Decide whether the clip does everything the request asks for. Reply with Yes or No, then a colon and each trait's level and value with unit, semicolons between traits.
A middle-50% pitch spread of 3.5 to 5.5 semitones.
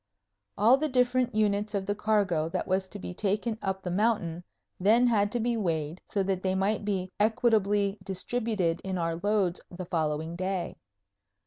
No: average, 3.1 semitones